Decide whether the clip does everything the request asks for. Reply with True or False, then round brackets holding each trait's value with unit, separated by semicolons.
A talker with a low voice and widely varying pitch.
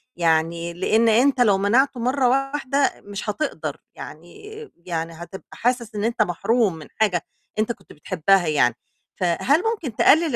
False (215 Hz; 6.8 semitones)